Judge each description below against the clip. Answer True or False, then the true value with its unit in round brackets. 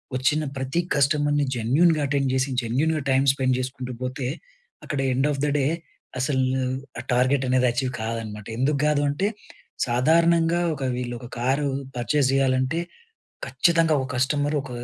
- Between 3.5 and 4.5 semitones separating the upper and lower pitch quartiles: False (2.6 semitones)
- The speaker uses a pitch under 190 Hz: True (135 Hz)